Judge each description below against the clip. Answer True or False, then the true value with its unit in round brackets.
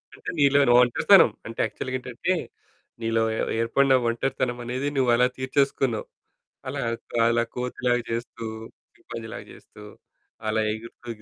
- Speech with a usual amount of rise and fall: False (2.1 semitones)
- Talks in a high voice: False (120 Hz)